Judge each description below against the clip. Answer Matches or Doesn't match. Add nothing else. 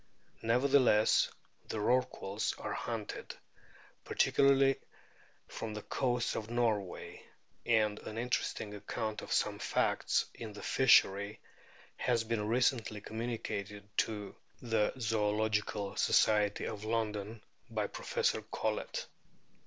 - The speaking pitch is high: Doesn't match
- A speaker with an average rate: Doesn't match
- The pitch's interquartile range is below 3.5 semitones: Matches